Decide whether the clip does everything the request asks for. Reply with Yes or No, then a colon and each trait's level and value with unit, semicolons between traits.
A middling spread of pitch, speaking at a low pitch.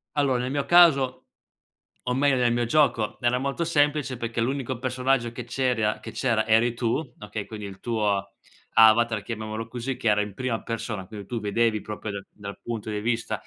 Yes: average, 3.0 semitones; low, 115 Hz